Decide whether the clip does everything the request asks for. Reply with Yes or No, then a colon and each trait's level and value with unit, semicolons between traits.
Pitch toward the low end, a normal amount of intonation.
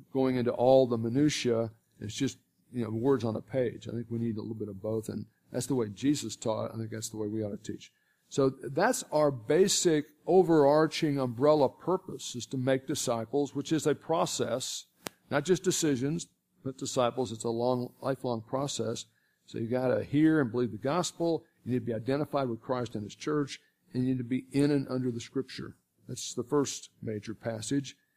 Yes: low, 130 Hz; average, 3.9 semitones